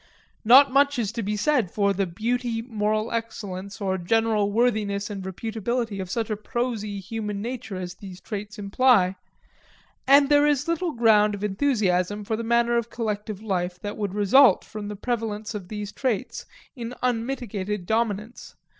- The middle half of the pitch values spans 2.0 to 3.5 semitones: Yes, average, 2.9 semitones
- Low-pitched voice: No, high, 215 Hz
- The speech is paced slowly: No, average, 165 wpm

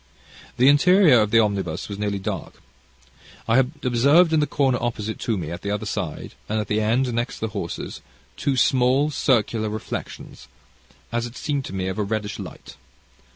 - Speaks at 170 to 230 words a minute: Yes, average, 185 wpm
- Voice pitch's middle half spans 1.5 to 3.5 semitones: No, average, 4.2 semitones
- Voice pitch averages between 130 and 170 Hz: No, low, 115 Hz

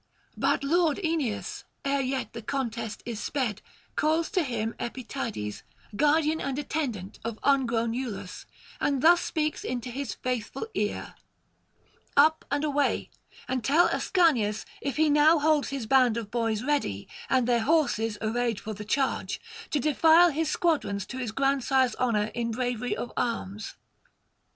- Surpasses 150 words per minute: No, average, 145 wpm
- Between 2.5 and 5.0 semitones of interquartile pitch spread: Yes, average, 4.6 semitones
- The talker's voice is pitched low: No, very high, 260 Hz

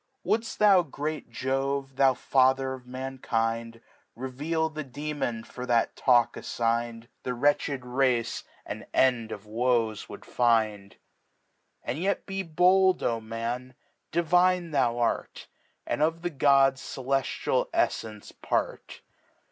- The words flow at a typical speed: No, slow, 120 wpm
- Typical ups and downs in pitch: Yes, average, 4.3 semitones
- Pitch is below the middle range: Yes, low, 130 Hz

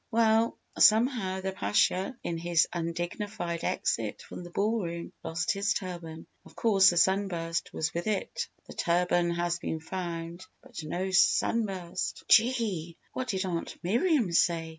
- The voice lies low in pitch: No, medium, 185 Hz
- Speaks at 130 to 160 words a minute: Yes, average, 145 wpm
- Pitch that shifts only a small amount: No, average, 3.9 semitones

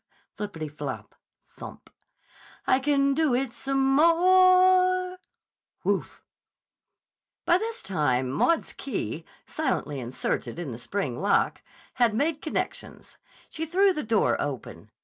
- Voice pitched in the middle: No, very high, 275 Hz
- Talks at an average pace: No, slow, 115 wpm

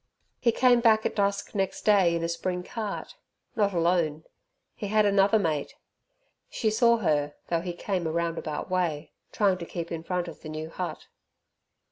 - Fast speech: No, average, 175 wpm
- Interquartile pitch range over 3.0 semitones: Yes, average, 3.6 semitones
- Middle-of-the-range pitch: Yes, medium, 180 Hz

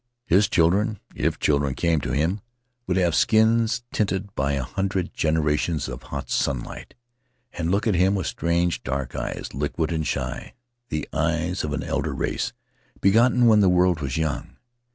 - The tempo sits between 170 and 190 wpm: Yes, average, 175 wpm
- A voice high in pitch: No, very low, 85 Hz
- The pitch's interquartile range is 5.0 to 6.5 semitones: Yes, average, 5.3 semitones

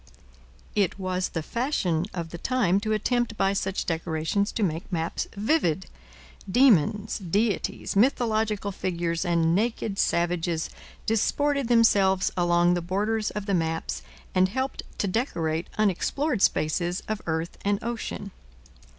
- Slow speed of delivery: Yes, slow, 130 wpm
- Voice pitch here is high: Yes, high, 195 Hz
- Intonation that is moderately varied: Yes, average, 4.1 semitones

